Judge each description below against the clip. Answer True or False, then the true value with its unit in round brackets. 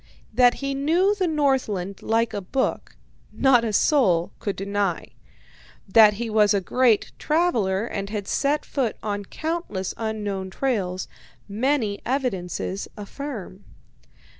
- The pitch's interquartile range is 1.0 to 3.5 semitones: False (5.4 semitones)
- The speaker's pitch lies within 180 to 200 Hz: False (220 Hz)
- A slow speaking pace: True (125 wpm)